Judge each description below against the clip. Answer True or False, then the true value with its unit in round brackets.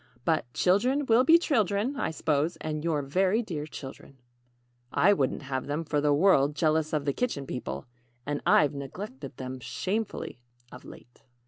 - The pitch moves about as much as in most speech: False (6.1 semitones)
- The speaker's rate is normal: True (160 wpm)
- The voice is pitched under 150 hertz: False (155 Hz)